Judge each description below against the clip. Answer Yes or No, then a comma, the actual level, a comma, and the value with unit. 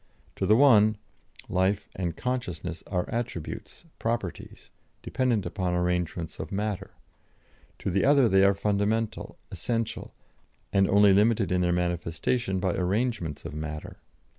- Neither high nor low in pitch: No, low, 100 Hz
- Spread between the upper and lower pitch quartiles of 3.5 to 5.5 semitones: Yes, average, 4.0 semitones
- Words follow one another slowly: Yes, slow, 130 wpm